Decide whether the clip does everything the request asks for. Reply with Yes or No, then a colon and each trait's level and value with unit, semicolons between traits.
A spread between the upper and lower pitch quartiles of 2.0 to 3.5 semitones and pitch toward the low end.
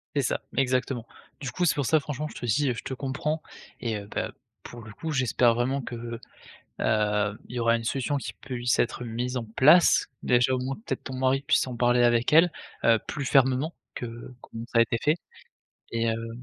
Yes: average, 2.9 semitones; low, 125 Hz